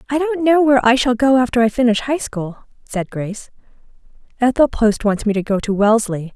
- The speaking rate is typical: No, fast, 210 wpm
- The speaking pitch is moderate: No, high, 235 Hz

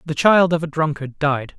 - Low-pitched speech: No, medium, 150 Hz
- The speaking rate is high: Yes, fast, 225 wpm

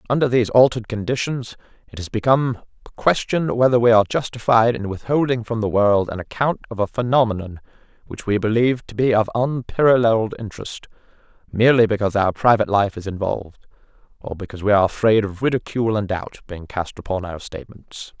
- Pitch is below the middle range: Yes, low, 110 Hz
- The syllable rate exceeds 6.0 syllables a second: Yes, 6.3 syllables/s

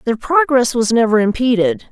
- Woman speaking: Yes, female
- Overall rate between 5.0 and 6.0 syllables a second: Yes, 5.1 syllables/s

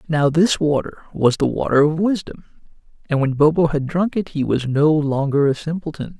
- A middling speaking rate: Yes, average, 195 wpm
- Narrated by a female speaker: No, male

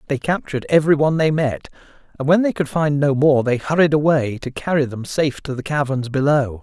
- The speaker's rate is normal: No, fast, 215 wpm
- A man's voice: Yes, male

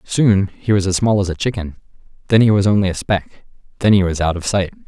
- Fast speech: Yes, fast, 245 wpm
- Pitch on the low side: Yes, very low, 95 Hz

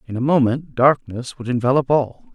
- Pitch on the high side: No, low, 130 Hz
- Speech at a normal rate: Yes, average, 180 wpm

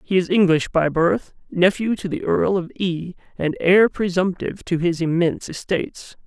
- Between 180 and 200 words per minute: No, average, 170 wpm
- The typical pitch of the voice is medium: Yes, medium, 180 Hz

